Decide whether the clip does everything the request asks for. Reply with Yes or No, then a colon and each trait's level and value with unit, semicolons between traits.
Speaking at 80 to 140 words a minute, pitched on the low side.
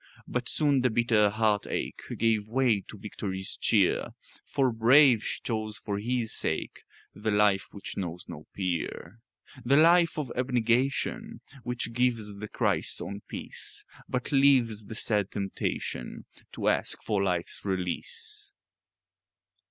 Yes: slow, 135 wpm; low, 115 Hz